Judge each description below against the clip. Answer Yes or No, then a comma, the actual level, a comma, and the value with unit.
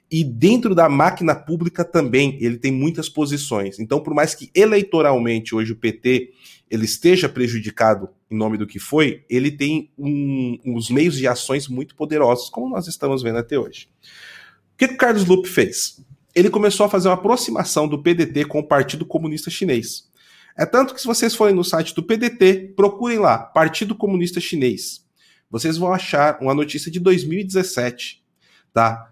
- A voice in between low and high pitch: Yes, medium, 155 Hz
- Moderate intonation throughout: No, wide, 6.4 semitones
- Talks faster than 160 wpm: Yes, average, 170 wpm